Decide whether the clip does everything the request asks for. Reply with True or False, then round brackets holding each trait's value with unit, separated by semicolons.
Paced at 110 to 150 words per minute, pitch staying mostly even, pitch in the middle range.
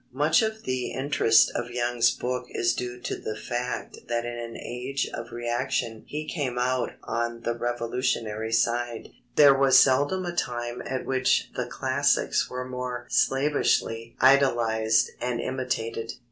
False (145 wpm; 1.8 semitones; 125 Hz)